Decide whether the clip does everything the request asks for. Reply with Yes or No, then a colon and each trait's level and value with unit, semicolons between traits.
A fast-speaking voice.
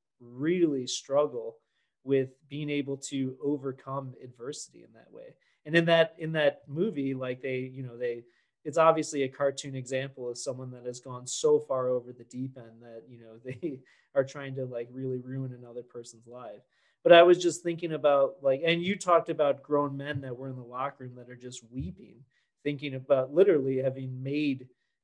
No: average, 190 wpm